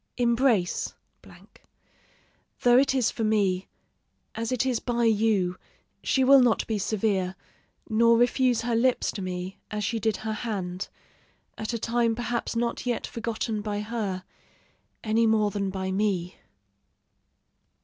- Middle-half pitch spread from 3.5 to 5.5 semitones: No, average, 2.9 semitones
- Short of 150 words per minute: Yes, average, 140 wpm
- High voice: Yes, high, 220 Hz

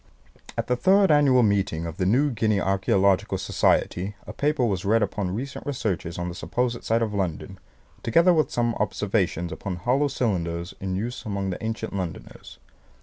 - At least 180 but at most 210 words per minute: No, average, 170 wpm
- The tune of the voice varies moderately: Yes, average, 4.6 semitones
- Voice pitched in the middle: No, low, 105 Hz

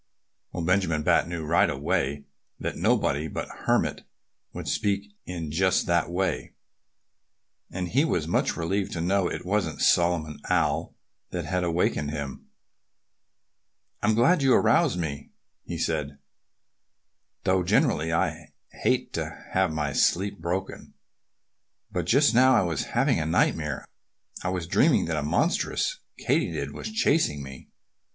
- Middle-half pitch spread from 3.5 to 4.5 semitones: Yes, average, 4.1 semitones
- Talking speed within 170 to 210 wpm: No, average, 145 wpm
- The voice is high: No, very low, 85 Hz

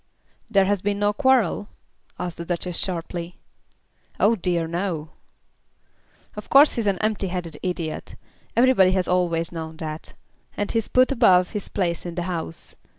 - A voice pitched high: No, medium, 180 Hz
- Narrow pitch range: No, average, 3.4 semitones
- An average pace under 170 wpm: Yes, average, 155 wpm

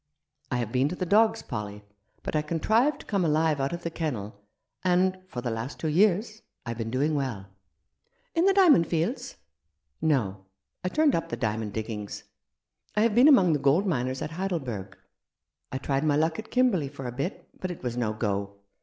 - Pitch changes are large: Yes, wide, 8.0 semitones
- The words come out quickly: Yes, fast, 210 wpm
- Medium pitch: Yes, medium, 150 Hz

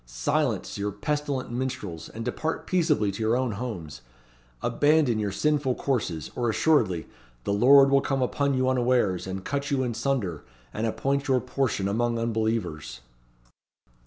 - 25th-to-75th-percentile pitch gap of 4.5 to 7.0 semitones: Yes, average, 5.3 semitones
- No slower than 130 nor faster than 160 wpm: Yes, average, 150 wpm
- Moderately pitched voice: No, low, 120 Hz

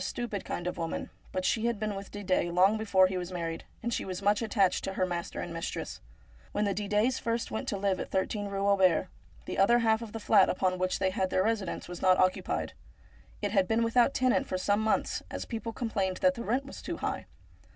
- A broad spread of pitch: No, average, 3.2 semitones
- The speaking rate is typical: No, fast, 235 wpm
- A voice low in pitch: No, high, 200 Hz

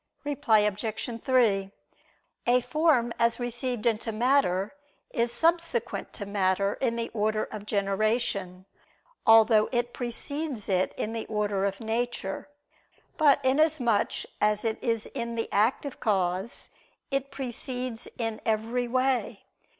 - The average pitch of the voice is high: Yes, high, 230 Hz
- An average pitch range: Yes, average, 3.0 semitones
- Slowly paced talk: Yes, slow, 125 wpm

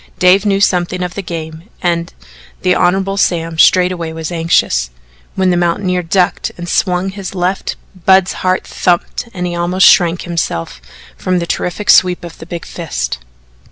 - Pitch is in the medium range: Yes, medium, 180 Hz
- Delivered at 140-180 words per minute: Yes, average, 160 wpm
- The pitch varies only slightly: Yes, narrow, 1.5 semitones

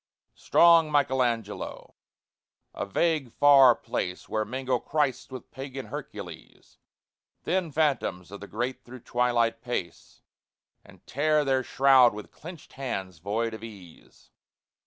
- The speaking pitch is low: Yes, low, 125 Hz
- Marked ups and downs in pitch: No, average, 4.3 semitones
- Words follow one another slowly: Yes, slow, 120 wpm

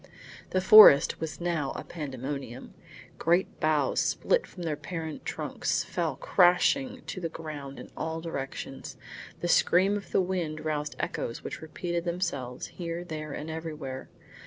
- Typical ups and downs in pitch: Yes, average, 3.2 semitones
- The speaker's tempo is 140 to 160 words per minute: Yes, average, 145 wpm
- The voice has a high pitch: No, medium, 160 Hz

